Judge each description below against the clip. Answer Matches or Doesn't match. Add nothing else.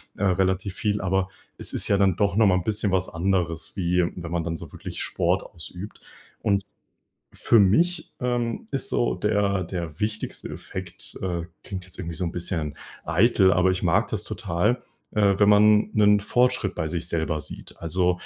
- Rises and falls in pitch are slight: Doesn't match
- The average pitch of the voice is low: Matches